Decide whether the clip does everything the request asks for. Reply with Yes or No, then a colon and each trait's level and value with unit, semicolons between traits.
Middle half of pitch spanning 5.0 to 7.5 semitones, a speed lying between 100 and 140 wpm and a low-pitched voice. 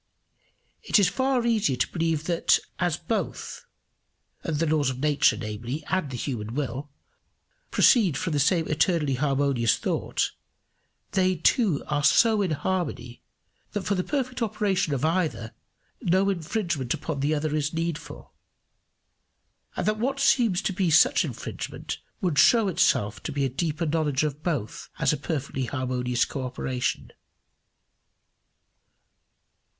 No: wide, 5.4 semitones; slow, 135 wpm; medium, 155 Hz